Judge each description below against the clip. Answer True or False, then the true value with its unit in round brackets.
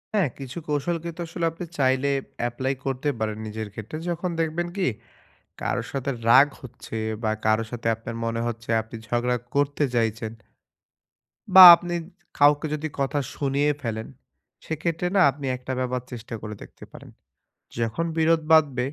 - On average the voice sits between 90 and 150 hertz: True (135 Hz)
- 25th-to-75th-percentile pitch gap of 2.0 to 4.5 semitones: False (5.3 semitones)